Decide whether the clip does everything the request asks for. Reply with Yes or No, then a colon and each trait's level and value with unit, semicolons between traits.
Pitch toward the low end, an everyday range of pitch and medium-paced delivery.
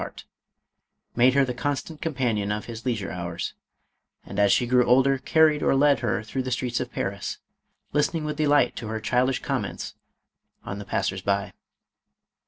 Yes: low, 125 Hz; average, 4.7 semitones; average, 180 wpm